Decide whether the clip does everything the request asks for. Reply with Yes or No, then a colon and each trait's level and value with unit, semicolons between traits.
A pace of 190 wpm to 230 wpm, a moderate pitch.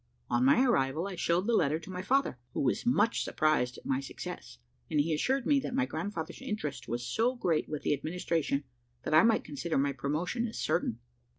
Yes: fast, 205 wpm; medium, 165 Hz